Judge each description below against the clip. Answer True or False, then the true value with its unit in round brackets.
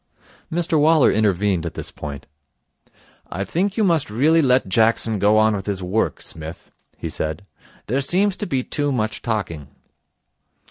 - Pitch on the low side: True (110 Hz)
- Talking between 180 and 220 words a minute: False (155 wpm)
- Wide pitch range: True (7.9 semitones)